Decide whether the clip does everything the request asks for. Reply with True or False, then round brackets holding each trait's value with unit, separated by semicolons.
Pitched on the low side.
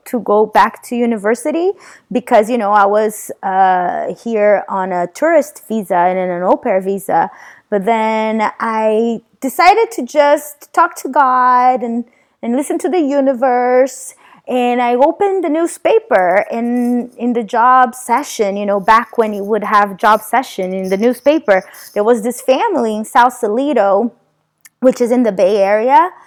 False (240 Hz)